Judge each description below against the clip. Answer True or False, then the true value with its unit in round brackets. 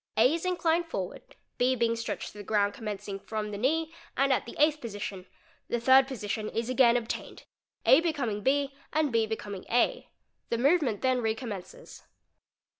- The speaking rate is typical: True (165 wpm)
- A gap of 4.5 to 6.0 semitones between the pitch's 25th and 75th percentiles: True (4.8 semitones)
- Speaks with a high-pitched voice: True (240 Hz)